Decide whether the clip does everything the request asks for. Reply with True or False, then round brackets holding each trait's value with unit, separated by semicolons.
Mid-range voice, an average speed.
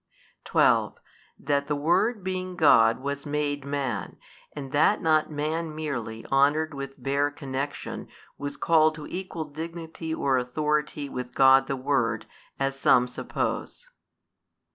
False (145 Hz; 130 wpm)